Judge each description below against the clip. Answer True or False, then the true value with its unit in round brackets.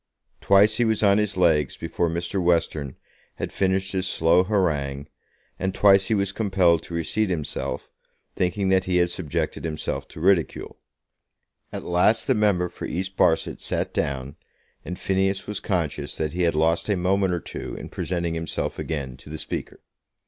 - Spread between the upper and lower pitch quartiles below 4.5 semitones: True (3.0 semitones)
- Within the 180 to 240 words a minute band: False (170 wpm)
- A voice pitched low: True (90 Hz)